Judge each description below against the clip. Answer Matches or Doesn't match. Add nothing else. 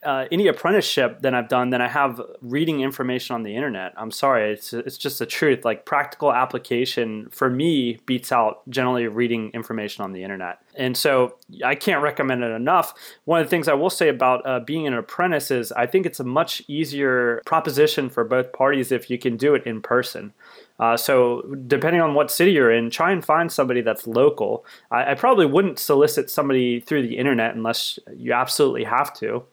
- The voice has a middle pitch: Doesn't match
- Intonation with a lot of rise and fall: Doesn't match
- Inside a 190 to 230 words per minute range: Matches